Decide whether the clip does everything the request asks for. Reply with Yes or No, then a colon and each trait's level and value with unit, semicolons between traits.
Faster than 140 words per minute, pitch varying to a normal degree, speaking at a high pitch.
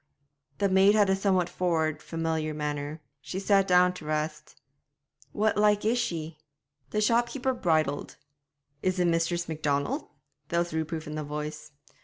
No: average, 150 wpm; average, 4.2 semitones; medium, 170 Hz